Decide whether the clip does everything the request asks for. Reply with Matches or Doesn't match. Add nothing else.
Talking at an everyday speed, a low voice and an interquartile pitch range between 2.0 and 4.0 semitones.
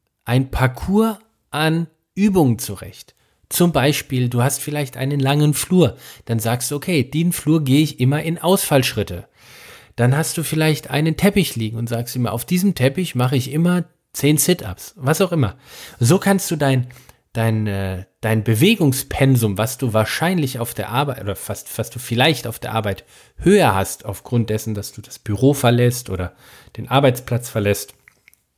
Doesn't match